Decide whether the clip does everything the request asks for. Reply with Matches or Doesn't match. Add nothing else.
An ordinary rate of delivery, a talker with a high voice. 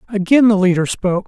Matches